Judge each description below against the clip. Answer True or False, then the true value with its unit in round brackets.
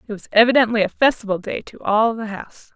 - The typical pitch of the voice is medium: False (220 Hz)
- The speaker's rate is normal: False (220 wpm)